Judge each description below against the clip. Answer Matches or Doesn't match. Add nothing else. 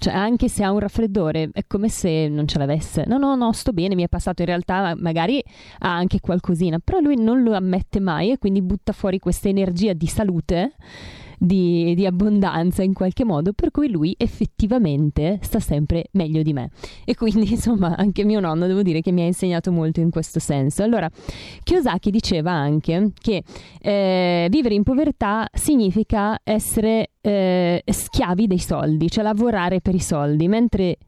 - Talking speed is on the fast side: Matches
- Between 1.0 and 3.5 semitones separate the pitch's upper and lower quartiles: Doesn't match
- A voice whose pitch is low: Doesn't match